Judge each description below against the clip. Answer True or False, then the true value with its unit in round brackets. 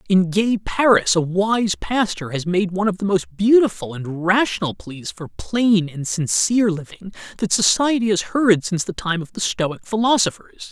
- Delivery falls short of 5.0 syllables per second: True (4.7 syllables/s)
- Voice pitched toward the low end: False (190 Hz)